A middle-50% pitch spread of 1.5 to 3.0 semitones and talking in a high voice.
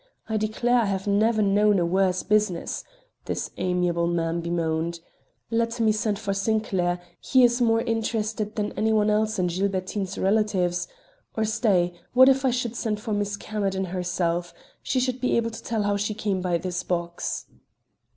No: average, 3.6 semitones; high, 205 Hz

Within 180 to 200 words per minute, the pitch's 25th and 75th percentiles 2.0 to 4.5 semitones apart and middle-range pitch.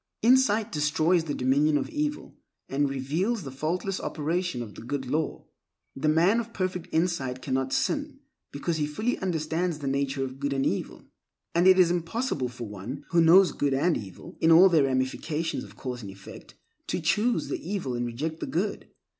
No: average, 185 wpm; average, 5.2 semitones; medium, 155 Hz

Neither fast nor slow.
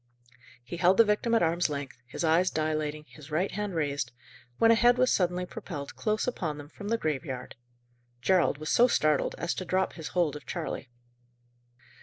Yes: average, 185 wpm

